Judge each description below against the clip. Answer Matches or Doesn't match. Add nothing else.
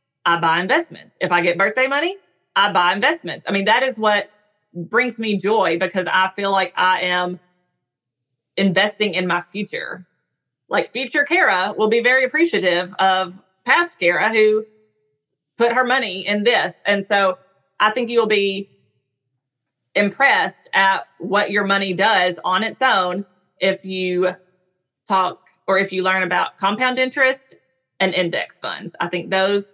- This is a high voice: Matches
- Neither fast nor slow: Matches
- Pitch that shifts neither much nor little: Matches